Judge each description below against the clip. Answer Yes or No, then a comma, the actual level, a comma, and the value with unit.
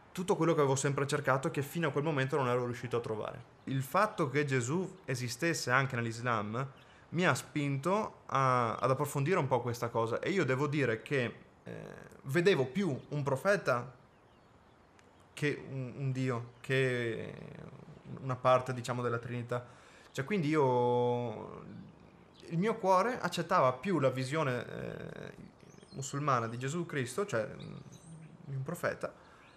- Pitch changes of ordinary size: Yes, average, 4.8 semitones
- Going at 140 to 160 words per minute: Yes, average, 145 wpm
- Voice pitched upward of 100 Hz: Yes, low, 135 Hz